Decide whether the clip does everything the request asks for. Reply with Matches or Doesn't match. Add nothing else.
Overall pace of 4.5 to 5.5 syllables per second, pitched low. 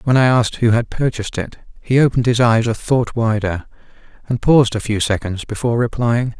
Doesn't match